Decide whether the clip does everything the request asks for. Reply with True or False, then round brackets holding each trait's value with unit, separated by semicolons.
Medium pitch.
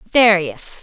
False (205 Hz)